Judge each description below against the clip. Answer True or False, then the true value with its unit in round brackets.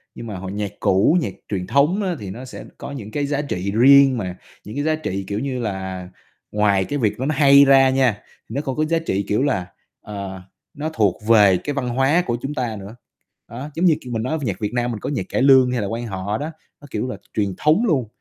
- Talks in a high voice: False (120 Hz)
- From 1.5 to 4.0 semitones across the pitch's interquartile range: False (5.6 semitones)